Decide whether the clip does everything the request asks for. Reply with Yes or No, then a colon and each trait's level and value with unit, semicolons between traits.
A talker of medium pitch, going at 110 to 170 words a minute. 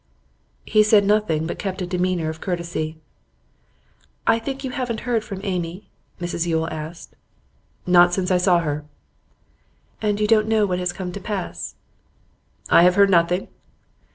Yes: medium, 180 Hz; average, 160 wpm